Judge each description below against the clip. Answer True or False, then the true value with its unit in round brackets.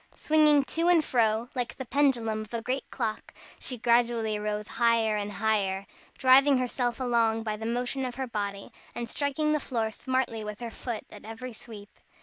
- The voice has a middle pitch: False (235 Hz)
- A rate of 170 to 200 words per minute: True (180 wpm)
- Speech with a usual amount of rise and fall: True (3.1 semitones)